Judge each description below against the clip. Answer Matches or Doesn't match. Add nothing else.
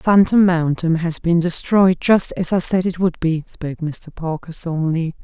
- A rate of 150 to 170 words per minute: Doesn't match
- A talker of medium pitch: Matches